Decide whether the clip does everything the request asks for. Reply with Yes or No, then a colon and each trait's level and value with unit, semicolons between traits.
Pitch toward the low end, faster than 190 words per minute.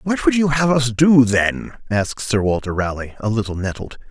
Yes: low, 120 Hz; fast, 205 wpm